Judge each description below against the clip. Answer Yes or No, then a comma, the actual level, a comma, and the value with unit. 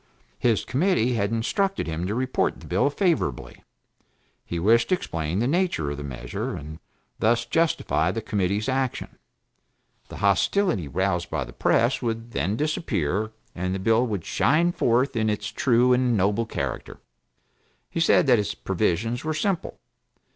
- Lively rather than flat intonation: Yes, wide, 5.7 semitones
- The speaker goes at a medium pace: Yes, average, 155 wpm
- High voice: No, low, 115 Hz